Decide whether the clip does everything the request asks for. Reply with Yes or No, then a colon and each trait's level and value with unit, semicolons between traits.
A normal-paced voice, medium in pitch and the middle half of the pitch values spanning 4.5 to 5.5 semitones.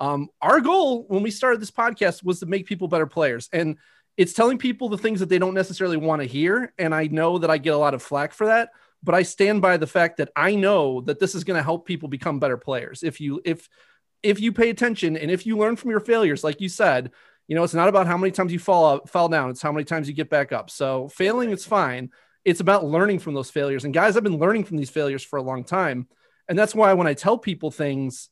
No: fast, 265 wpm; medium, 180 Hz; average, 5.1 semitones